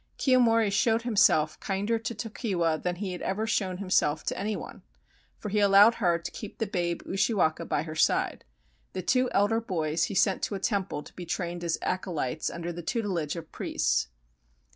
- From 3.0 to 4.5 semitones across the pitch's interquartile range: Yes, average, 4.1 semitones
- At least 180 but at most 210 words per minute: Yes, average, 185 wpm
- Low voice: No, high, 190 Hz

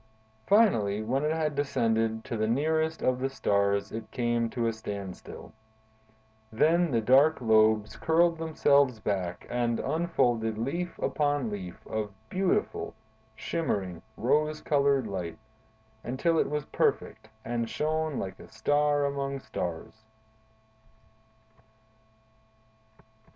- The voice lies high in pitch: No, low, 125 Hz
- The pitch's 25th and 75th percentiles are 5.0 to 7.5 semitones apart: Yes, wide, 5.6 semitones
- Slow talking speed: Yes, slow, 115 wpm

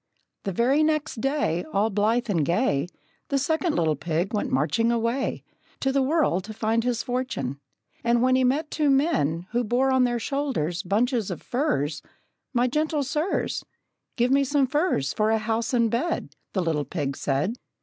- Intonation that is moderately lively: No, wide, 6.7 semitones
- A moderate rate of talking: Yes, average, 175 wpm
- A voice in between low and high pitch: No, high, 235 Hz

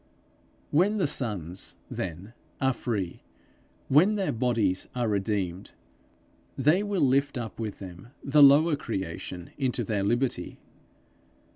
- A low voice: Yes, low, 120 Hz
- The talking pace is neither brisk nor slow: No, slow, 120 wpm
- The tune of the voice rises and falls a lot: Yes, wide, 6.5 semitones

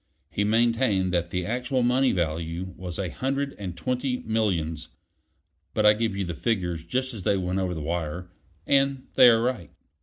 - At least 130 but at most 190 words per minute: Yes, average, 180 wpm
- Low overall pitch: Yes, low, 100 Hz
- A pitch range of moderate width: No, wide, 6.0 semitones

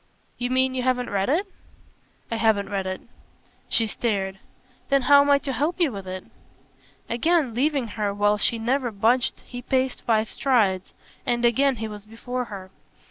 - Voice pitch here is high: Yes, high, 235 Hz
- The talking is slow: No, average, 175 wpm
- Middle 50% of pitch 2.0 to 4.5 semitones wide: Yes, average, 4.1 semitones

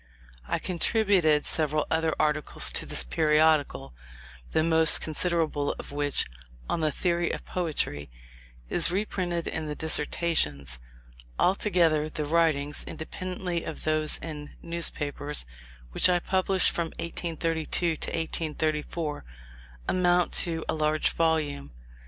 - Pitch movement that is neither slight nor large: No, narrow, 2.2 semitones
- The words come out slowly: Yes, slow, 115 wpm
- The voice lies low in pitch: No, medium, 160 Hz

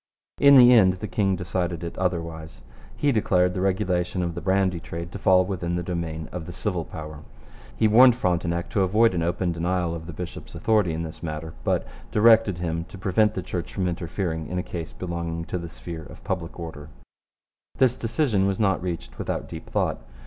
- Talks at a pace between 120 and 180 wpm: No, average, 200 wpm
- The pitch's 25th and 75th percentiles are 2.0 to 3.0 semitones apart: Yes, narrow, 2.5 semitones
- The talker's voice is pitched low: Yes, very low, 90 Hz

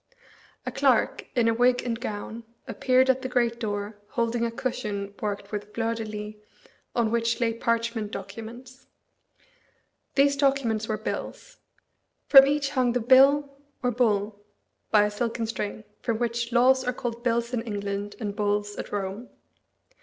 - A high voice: Yes, high, 230 Hz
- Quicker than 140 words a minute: Yes, average, 155 wpm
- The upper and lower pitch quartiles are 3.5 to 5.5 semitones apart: No, average, 3.0 semitones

